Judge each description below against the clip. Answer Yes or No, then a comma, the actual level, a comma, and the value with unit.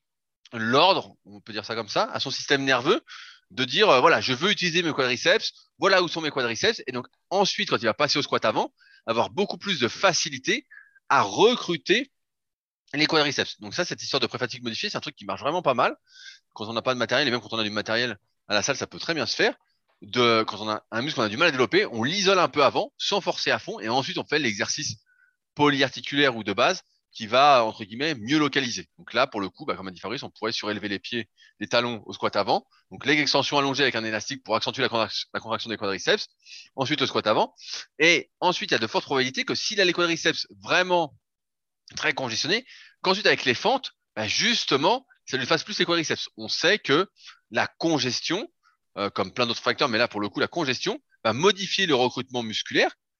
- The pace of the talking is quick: Yes, fast, 230 wpm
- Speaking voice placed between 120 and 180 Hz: Yes, low, 135 Hz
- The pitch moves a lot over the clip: Yes, wide, 7.9 semitones